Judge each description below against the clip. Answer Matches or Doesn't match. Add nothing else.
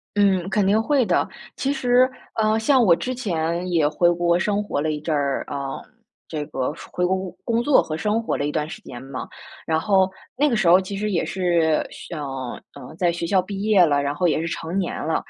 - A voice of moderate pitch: Matches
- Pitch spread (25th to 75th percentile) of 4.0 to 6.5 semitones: Matches